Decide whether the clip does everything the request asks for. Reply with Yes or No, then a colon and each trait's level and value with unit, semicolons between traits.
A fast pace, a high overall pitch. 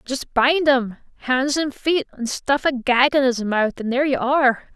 Yes: fast, 215 wpm; very high, 260 Hz